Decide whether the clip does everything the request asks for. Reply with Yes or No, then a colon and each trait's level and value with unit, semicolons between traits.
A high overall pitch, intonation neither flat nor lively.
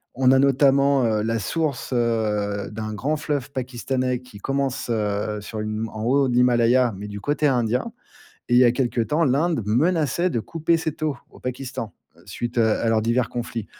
No: low, 125 Hz; average, 3.7 semitones